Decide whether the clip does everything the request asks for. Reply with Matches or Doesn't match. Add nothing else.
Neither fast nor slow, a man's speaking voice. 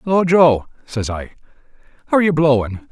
Matches